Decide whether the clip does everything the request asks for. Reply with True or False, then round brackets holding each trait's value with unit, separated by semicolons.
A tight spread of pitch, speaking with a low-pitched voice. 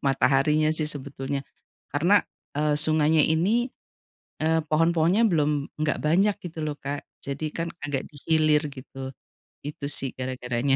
False (2.3 semitones; 150 Hz)